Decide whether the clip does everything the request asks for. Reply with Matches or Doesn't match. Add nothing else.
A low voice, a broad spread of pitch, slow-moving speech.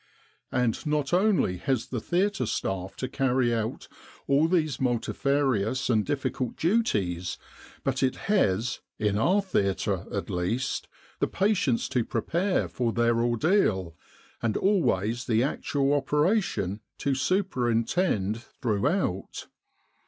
Matches